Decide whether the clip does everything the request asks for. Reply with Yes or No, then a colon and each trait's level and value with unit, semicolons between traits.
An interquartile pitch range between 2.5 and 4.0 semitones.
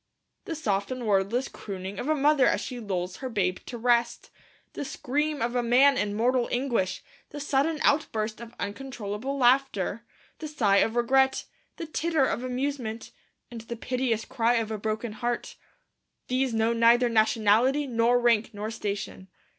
Yes: average, 3.4 semitones